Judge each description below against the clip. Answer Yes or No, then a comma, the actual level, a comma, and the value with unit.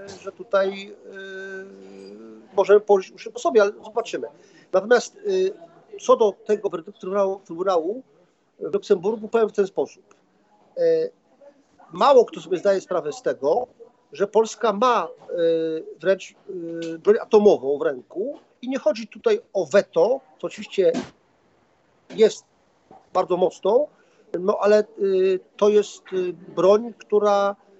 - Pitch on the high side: Yes, high, 210 Hz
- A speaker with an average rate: Yes, average, 130 wpm